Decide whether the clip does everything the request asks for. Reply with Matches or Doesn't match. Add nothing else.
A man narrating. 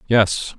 Matches